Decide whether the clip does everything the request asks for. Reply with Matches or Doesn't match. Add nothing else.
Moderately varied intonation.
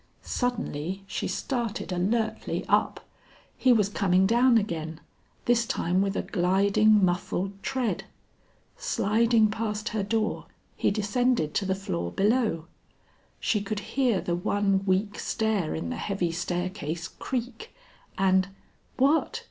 Matches